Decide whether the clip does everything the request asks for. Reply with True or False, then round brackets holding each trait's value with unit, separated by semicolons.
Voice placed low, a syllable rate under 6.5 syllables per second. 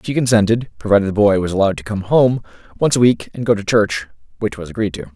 False (105 Hz; 6.8 syllables/s)